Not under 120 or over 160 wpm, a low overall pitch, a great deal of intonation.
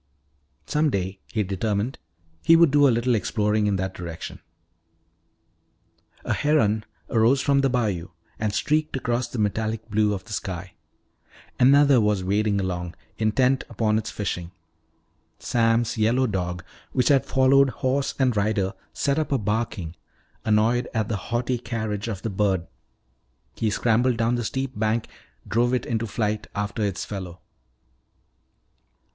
No: average, 145 wpm; low, 110 Hz; average, 3.5 semitones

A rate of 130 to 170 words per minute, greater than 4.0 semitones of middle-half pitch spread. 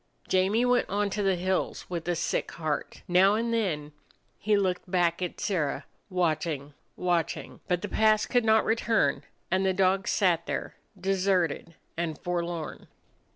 No: average, 155 wpm; average, 3.1 semitones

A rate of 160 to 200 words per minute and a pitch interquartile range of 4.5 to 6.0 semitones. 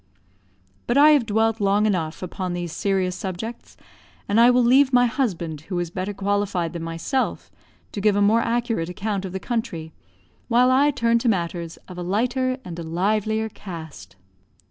Yes: average, 175 wpm; average, 4.9 semitones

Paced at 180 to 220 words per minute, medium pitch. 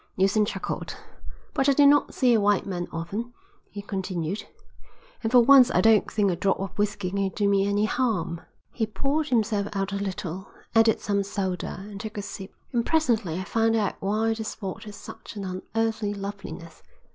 No: average, 190 wpm; high, 205 Hz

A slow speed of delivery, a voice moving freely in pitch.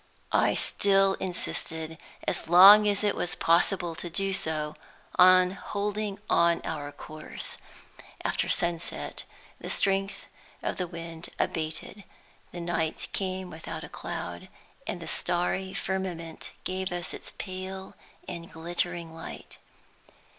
No: slow, 125 wpm; narrow, 2.6 semitones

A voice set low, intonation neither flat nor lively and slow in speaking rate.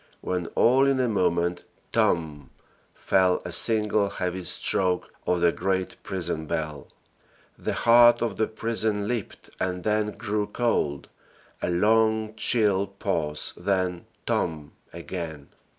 Yes: very low, 95 Hz; average, 4.1 semitones; slow, 125 wpm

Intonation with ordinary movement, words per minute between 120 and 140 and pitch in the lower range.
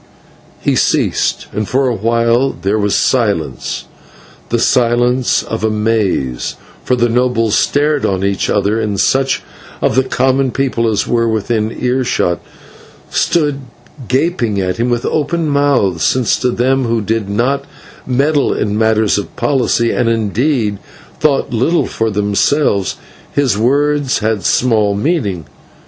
Yes: average, 4.0 semitones; slow, 135 wpm; low, 115 Hz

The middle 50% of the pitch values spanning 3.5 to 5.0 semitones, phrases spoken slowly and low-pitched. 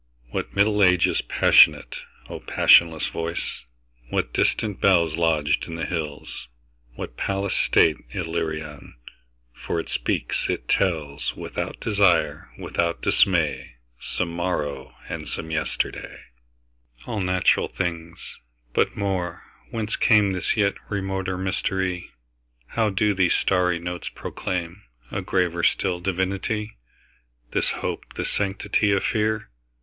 Yes: average, 4.3 semitones; slow, 95 wpm; very low, 90 Hz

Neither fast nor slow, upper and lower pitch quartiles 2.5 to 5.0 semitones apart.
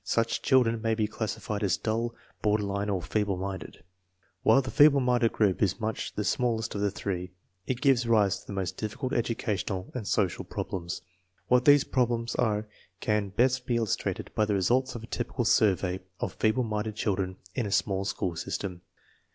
Yes: average, 185 wpm; average, 3.3 semitones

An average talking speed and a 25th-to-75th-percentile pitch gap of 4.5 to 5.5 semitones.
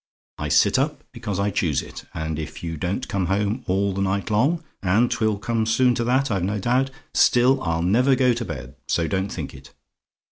No: fast, 210 wpm; average, 5.1 semitones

